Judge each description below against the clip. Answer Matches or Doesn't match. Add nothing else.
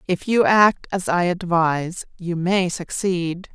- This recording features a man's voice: Doesn't match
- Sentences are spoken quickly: Doesn't match